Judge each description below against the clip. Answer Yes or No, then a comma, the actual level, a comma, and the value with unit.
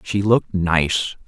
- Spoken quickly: No, average, 140 wpm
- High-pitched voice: No, very low, 95 Hz